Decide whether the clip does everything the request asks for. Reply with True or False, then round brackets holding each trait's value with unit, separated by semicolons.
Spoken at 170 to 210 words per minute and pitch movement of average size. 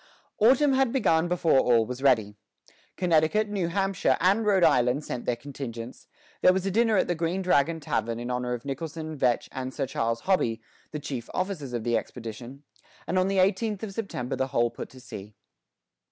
False (190 wpm; 7.4 semitones)